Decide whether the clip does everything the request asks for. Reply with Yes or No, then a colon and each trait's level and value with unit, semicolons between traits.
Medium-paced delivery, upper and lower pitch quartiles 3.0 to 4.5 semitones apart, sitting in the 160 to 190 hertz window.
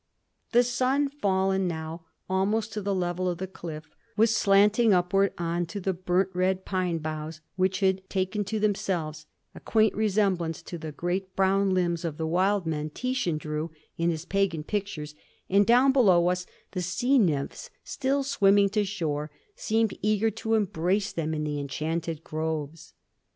Yes: average, 165 wpm; average, 3.8 semitones; medium, 185 Hz